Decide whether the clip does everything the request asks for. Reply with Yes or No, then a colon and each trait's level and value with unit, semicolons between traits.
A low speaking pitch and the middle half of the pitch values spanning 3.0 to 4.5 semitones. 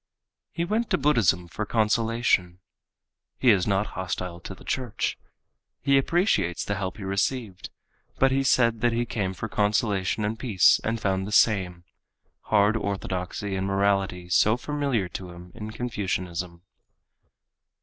Yes: low, 105 Hz; average, 3.9 semitones